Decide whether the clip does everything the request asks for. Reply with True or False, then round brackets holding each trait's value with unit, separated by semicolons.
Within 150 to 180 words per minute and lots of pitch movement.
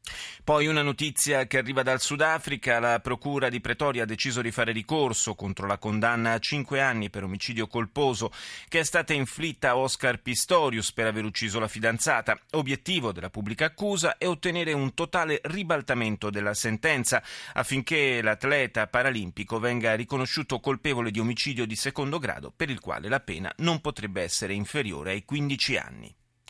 False (160 wpm; 4.7 semitones)